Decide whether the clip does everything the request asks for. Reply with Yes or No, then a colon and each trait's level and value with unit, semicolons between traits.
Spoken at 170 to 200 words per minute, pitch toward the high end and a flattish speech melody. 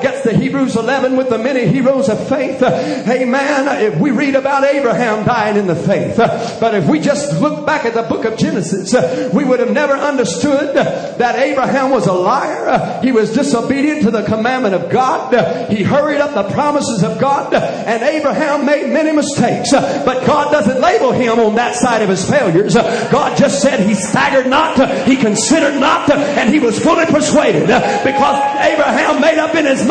No: average, 190 wpm; very high, 260 Hz; average, 3.9 semitones